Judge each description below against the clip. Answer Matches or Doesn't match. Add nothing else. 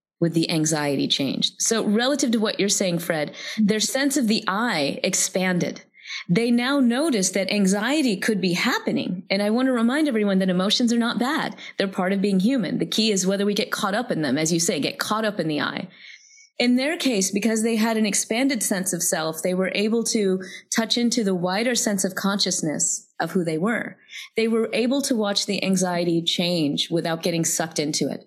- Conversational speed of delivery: Doesn't match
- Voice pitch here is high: Matches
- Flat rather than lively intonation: Doesn't match